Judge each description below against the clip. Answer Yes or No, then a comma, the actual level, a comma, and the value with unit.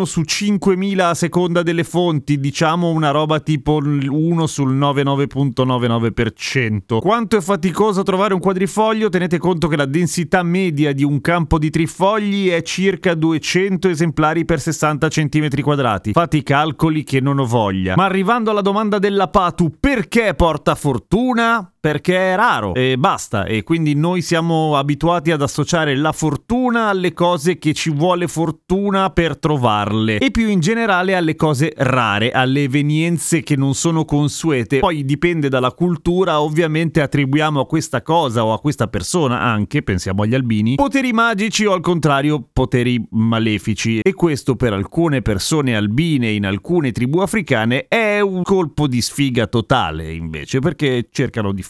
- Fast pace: No, average, 155 wpm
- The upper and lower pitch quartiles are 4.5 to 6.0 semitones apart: Yes, average, 5.1 semitones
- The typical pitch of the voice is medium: Yes, medium, 155 Hz